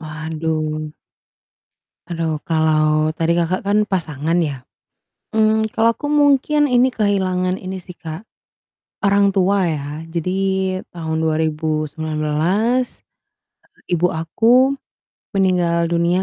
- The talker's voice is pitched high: No, medium, 170 Hz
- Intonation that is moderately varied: Yes, average, 4.3 semitones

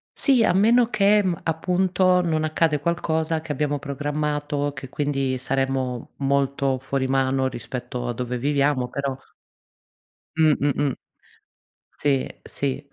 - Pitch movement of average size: Yes, average, 3.1 semitones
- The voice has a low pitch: No, medium, 145 Hz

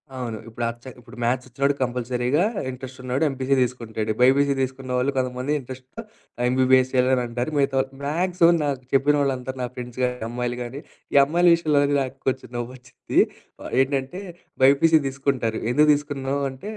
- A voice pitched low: Yes, low, 130 Hz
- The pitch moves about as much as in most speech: No, narrow, 2.0 semitones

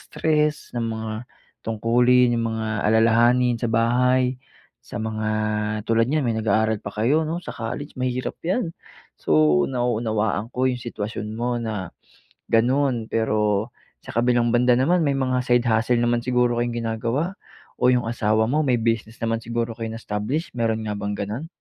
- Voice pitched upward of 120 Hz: No, low, 115 Hz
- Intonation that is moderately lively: No, narrow, 2.2 semitones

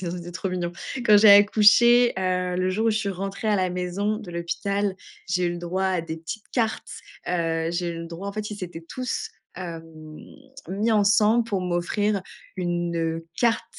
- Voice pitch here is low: No, medium, 185 Hz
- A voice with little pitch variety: No, average, 3.3 semitones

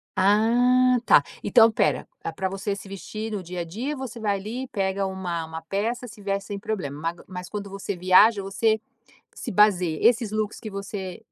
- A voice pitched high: Yes, high, 200 Hz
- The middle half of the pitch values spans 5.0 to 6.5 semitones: No, average, 2.8 semitones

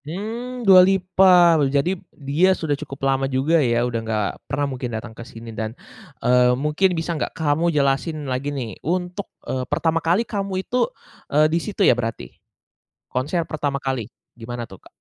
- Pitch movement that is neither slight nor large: No, wide, 6.0 semitones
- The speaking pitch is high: No, medium, 145 Hz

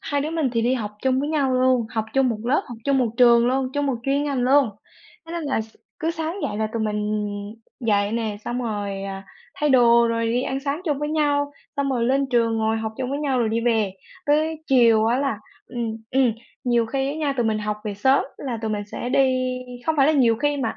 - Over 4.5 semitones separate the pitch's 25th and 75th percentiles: No, average, 3.8 semitones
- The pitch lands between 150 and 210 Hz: No, very high, 250 Hz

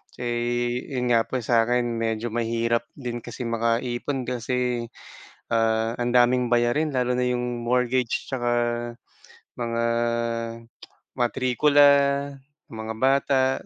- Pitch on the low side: Yes, low, 120 Hz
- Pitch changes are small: Yes, narrow, 1.2 semitones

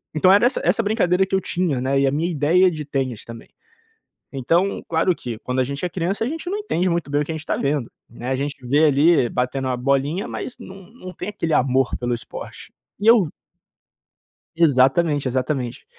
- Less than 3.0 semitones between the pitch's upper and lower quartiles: No, wide, 5.6 semitones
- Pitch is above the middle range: No, medium, 150 Hz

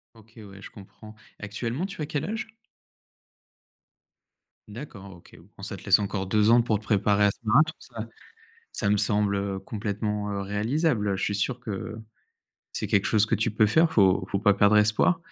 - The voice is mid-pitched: No, low, 105 Hz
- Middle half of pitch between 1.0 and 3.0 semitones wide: Yes, narrow, 2.4 semitones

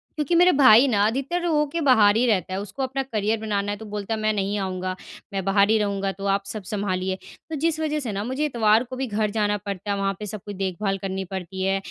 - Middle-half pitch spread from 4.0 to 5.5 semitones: Yes, average, 4.5 semitones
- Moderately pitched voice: No, high, 210 Hz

